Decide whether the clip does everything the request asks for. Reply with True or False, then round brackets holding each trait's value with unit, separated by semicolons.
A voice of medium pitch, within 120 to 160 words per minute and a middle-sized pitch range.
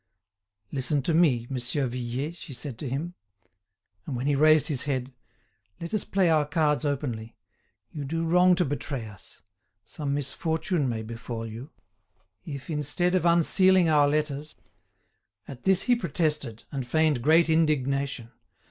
True (145 Hz; 150 wpm; 3.9 semitones)